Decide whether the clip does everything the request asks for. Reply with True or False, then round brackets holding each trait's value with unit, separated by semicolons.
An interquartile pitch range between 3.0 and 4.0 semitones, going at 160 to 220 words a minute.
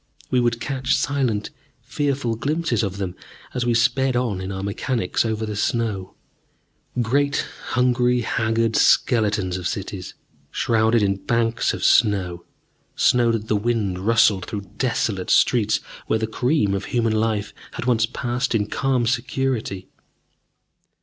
False (3.3 semitones; 140 wpm)